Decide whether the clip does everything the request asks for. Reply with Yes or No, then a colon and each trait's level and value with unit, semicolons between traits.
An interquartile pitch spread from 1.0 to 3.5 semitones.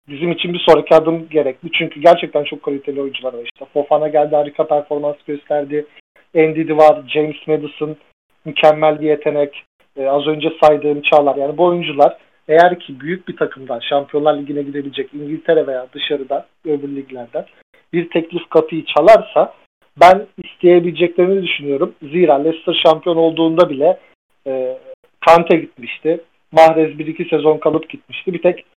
Yes: narrow, 2.4 semitones